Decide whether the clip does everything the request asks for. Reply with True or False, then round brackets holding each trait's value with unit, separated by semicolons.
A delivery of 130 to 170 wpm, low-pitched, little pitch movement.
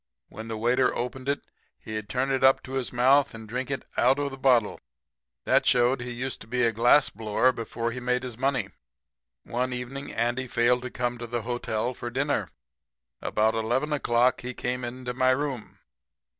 False (185 wpm; 125 Hz; 1.8 semitones)